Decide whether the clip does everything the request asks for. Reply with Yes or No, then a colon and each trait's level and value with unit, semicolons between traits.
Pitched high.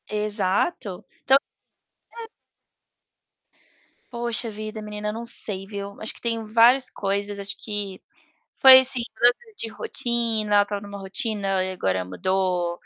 Yes: high, 210 Hz